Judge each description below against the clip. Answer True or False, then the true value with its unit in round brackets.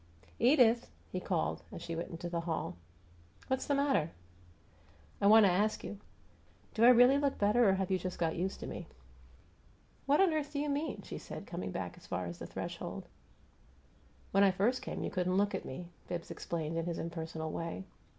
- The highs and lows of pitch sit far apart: True (6.7 semitones)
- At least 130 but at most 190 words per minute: False (200 wpm)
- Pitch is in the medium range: False (195 Hz)